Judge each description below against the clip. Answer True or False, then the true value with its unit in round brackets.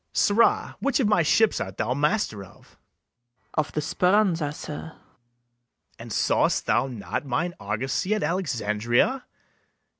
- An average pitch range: False (8.6 semitones)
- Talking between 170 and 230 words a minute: False (140 wpm)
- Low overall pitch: False (155 Hz)